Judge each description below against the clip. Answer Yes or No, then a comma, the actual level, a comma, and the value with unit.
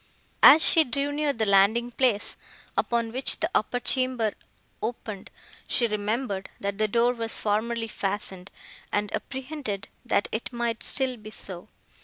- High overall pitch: Yes, high, 230 Hz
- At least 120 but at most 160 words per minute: Yes, average, 145 wpm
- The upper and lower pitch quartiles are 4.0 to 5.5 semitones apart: No, average, 3.6 semitones